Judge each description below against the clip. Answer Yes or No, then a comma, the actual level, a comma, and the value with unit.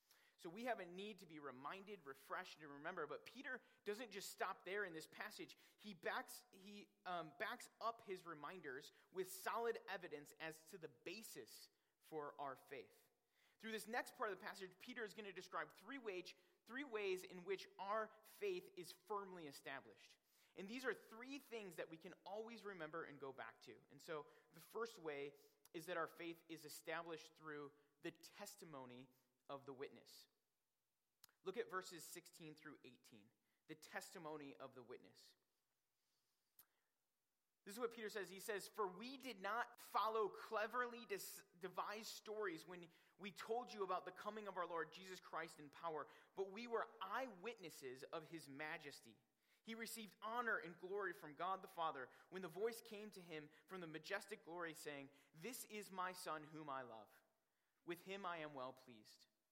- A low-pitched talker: No, medium, 185 Hz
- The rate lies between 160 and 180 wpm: Yes, average, 175 wpm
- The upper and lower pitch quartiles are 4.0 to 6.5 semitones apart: Yes, wide, 5.4 semitones